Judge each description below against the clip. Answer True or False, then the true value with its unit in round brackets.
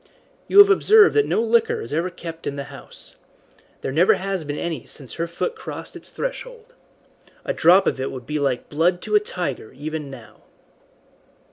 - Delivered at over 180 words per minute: True (190 wpm)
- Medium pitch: True (170 Hz)